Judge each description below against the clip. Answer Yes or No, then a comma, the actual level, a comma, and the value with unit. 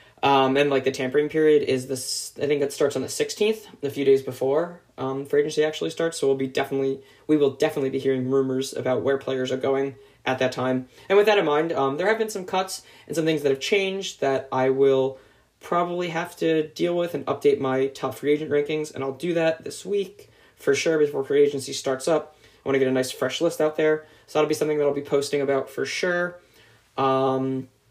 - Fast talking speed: Yes, fast, 235 wpm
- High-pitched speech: No, medium, 140 Hz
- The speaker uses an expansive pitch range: No, average, 3.8 semitones